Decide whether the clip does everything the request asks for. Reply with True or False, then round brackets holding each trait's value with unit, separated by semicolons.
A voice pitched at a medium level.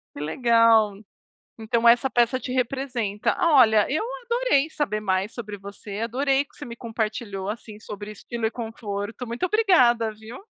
False (230 Hz)